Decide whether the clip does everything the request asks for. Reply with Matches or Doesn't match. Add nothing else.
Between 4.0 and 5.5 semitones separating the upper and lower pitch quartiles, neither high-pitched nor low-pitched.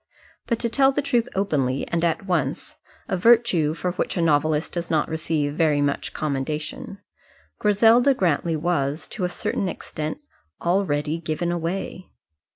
Matches